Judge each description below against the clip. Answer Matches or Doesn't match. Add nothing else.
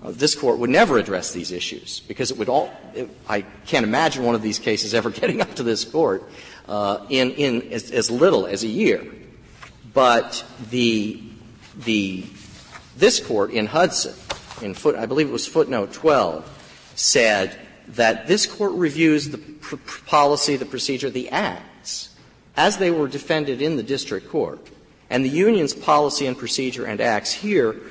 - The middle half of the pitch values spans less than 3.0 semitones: Doesn't match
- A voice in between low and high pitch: Doesn't match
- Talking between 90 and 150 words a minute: Doesn't match